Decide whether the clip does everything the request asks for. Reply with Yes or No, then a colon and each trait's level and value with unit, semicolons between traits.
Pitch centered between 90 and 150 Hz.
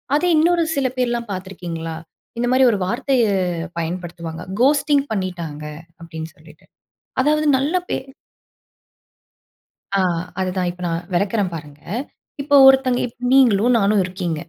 No: high, 200 Hz